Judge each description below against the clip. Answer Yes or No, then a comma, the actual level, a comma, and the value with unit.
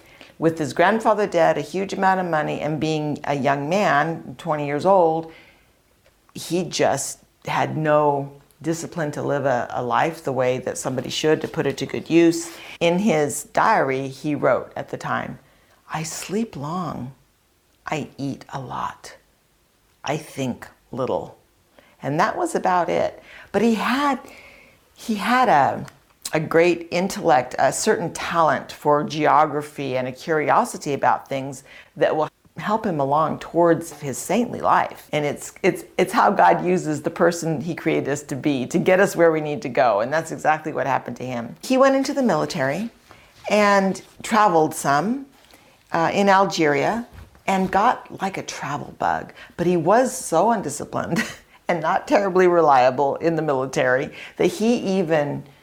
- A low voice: No, medium, 160 Hz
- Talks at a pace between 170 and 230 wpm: No, average, 160 wpm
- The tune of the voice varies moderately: Yes, average, 5.0 semitones